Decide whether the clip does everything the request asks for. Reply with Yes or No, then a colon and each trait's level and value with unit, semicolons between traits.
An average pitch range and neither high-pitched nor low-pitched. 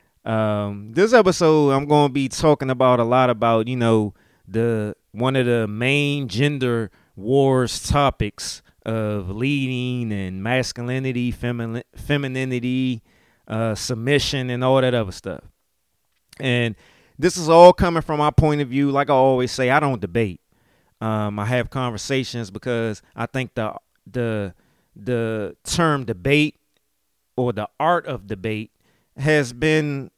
No: average, 3.9 semitones; low, 125 Hz